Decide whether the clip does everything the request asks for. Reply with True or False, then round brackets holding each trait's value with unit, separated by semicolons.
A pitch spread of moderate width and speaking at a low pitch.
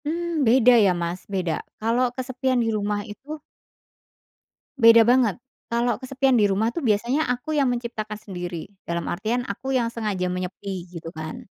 False (4.7 semitones; 230 Hz)